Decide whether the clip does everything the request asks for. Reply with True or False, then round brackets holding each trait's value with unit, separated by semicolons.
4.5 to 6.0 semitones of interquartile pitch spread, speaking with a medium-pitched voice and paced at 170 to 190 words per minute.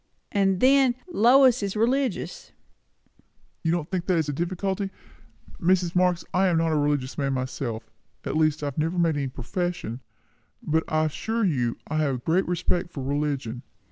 True (4.8 semitones; 165 Hz; 175 wpm)